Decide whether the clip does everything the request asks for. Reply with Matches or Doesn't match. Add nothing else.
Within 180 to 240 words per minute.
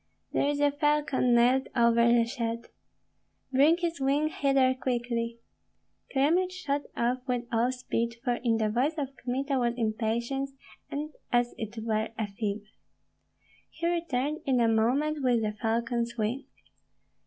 Doesn't match